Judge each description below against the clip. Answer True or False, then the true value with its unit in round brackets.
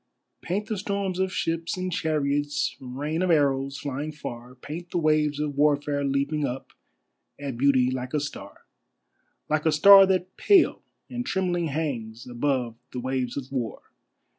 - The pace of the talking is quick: False (155 wpm)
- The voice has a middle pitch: True (145 Hz)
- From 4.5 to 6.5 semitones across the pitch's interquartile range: False (4.0 semitones)